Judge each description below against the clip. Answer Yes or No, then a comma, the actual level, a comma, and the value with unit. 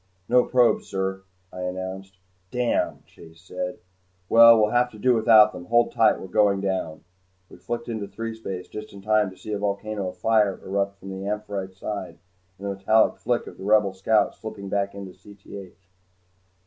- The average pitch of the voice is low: Yes, low, 100 Hz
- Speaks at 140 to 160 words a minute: No, average, 175 wpm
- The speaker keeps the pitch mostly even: Yes, narrow, 2.3 semitones